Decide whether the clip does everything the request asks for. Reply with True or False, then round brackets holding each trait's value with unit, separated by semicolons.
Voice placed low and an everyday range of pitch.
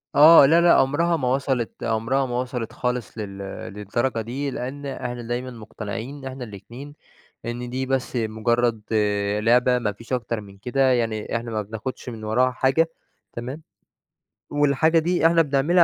True (125 Hz; 3.1 semitones)